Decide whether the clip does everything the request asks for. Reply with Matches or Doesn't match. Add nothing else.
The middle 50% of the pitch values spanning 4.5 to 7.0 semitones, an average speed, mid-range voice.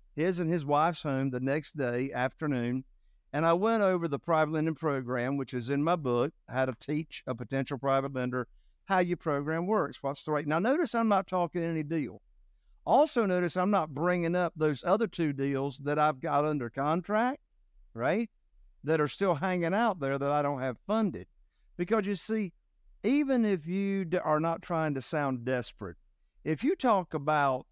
Matches